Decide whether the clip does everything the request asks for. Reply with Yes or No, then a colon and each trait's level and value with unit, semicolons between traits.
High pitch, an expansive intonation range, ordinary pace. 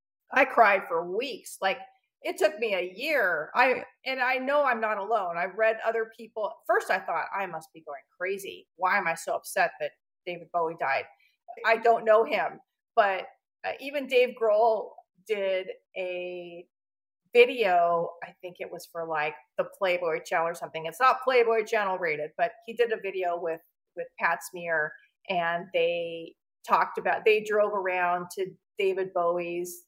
Yes: high, 195 Hz; wide, 6.0 semitones; average, 170 wpm